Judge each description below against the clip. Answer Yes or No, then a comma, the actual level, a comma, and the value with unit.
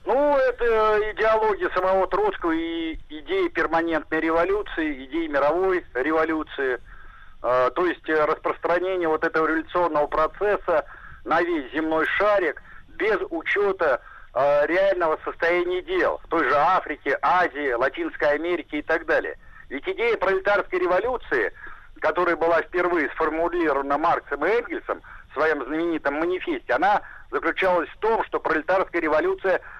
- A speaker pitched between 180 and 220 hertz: Yes, high, 190 Hz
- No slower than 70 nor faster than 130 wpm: Yes, average, 120 wpm